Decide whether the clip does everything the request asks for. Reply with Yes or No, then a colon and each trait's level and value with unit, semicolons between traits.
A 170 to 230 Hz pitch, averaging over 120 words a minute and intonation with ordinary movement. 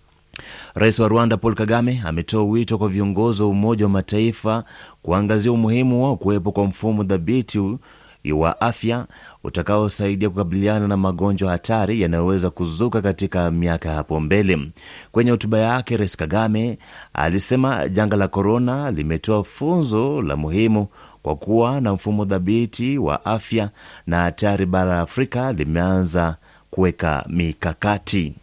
No: low, 105 Hz; average, 130 wpm; average, 3.8 semitones